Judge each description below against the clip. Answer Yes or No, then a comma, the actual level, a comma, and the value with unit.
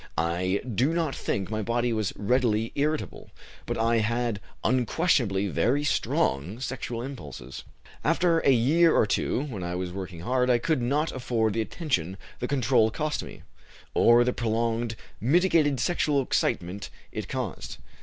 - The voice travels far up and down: No, average, 4.8 semitones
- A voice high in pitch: No, low, 120 Hz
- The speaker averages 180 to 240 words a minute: No, average, 150 wpm